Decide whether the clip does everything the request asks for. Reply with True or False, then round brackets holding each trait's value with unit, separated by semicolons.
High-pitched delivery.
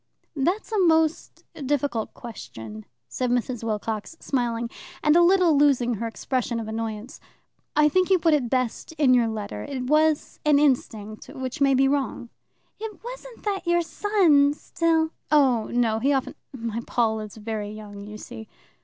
True (265 Hz)